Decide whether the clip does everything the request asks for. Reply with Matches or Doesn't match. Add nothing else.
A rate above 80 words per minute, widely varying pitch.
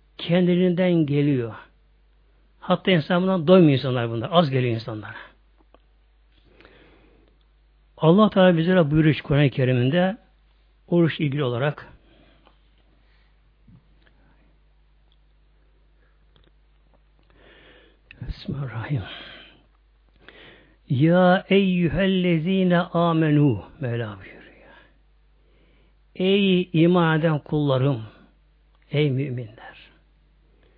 Doesn't match